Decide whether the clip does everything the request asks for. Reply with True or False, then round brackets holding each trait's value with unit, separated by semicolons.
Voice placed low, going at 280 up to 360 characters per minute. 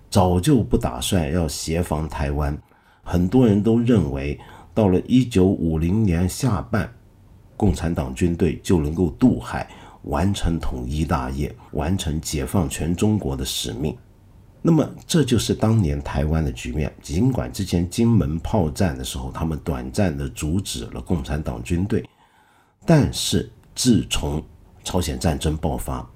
False (90 Hz; 225 characters per minute)